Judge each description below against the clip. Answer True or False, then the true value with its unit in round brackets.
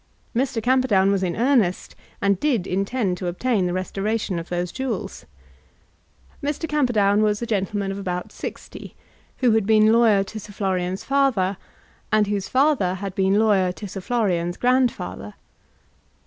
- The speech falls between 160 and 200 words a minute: False (150 wpm)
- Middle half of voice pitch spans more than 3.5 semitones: True (4.1 semitones)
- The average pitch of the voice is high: True (205 Hz)